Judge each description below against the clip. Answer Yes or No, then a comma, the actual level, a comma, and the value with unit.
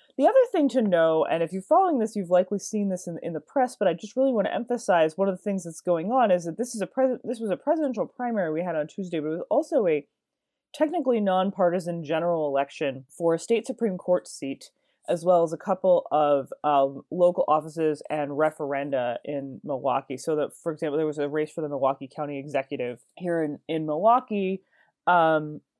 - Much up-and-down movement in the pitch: Yes, wide, 6.3 semitones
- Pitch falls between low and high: Yes, medium, 175 Hz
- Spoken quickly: Yes, fast, 215 wpm